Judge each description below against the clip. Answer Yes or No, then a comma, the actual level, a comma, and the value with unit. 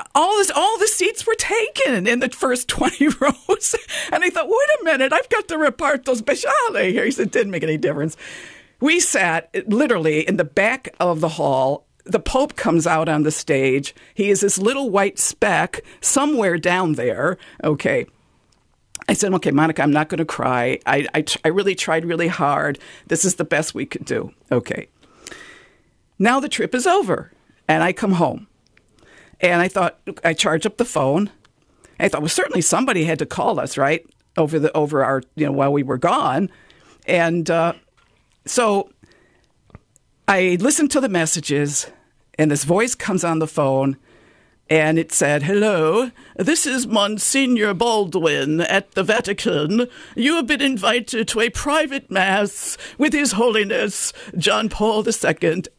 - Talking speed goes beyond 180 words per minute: No, average, 170 wpm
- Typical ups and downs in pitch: No, wide, 8.4 semitones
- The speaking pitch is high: Yes, high, 200 Hz